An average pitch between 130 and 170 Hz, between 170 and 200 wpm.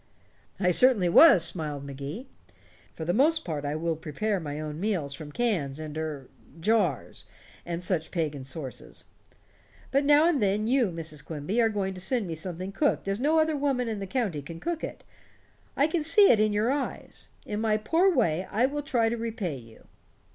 No: high, 195 Hz; average, 195 wpm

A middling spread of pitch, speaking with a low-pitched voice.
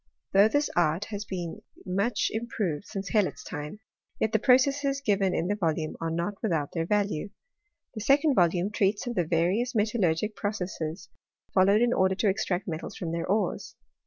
No: average, 4.1 semitones; high, 200 Hz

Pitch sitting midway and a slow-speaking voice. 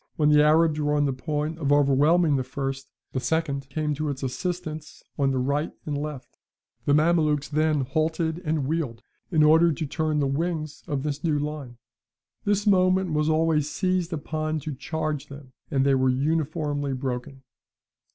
No: medium, 150 Hz; average, 170 wpm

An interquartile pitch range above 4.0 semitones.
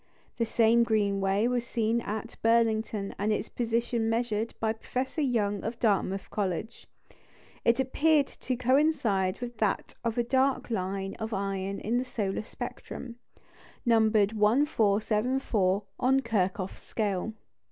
No: average, 3.0 semitones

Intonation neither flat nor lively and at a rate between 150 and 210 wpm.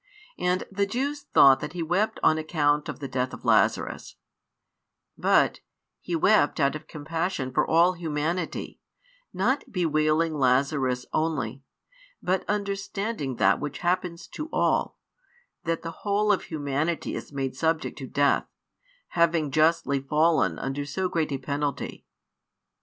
No: average, 4.0 semitones; average, 140 wpm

